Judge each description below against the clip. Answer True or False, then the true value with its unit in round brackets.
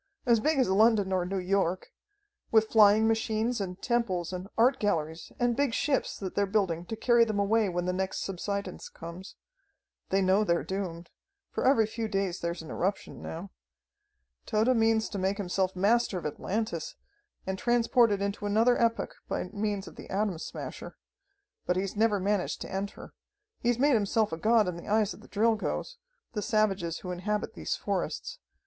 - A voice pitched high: True (205 Hz)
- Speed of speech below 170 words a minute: False (180 wpm)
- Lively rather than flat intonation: False (3.1 semitones)